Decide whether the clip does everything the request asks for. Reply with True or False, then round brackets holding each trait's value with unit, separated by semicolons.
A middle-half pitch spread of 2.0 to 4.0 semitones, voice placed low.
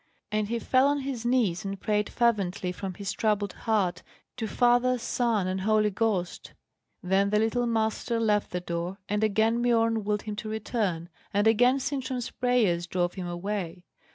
False (3.6 semitones; 215 Hz)